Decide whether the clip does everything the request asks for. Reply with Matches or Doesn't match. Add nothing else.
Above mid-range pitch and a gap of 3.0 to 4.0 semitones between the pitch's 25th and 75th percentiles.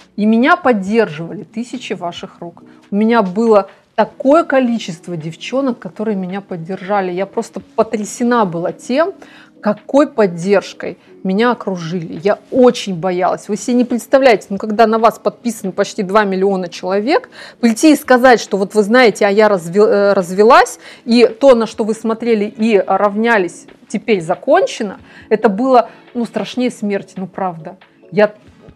Matches